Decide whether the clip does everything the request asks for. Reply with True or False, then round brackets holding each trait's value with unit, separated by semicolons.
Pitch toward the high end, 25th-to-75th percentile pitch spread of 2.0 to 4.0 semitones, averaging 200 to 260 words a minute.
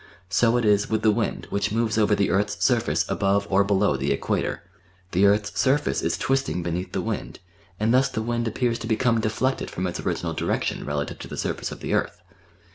False (105 Hz; 3.0 semitones; 205 wpm)